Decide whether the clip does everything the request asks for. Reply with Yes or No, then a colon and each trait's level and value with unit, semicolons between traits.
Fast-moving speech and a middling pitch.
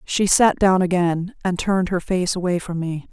Yes: fast, 210 wpm; medium, 180 Hz